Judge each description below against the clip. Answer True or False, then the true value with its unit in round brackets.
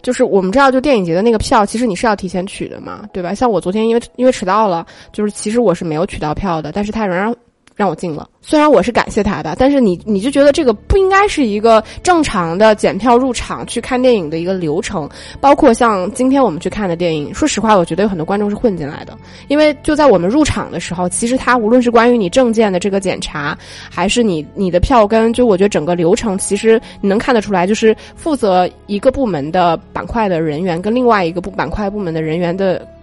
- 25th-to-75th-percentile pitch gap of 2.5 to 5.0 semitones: False (5.4 semitones)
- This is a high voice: True (210 Hz)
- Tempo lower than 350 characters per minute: False (370 characters per minute)